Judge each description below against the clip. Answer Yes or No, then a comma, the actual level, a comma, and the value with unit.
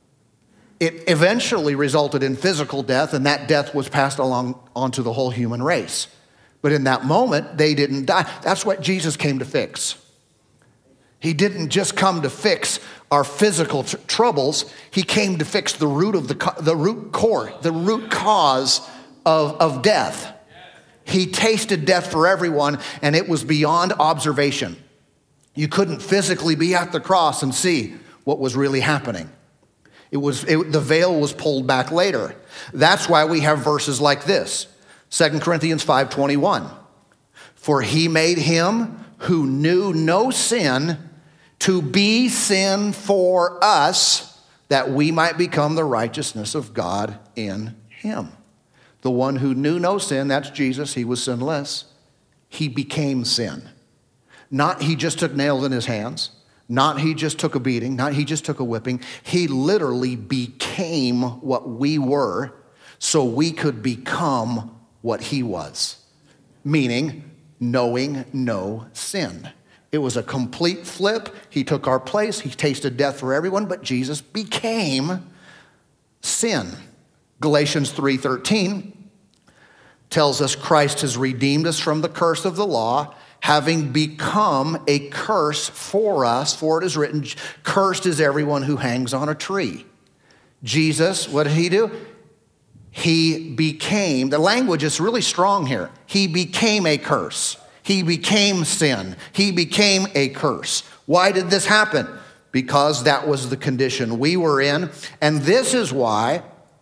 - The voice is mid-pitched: Yes, medium, 150 Hz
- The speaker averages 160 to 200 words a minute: No, average, 150 wpm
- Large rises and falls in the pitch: No, average, 4.5 semitones